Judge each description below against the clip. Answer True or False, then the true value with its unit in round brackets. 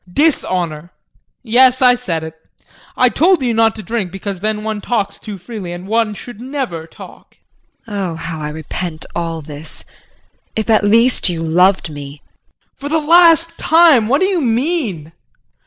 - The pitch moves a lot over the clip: True (6.7 semitones)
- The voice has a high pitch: True (215 Hz)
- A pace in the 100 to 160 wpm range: False (170 wpm)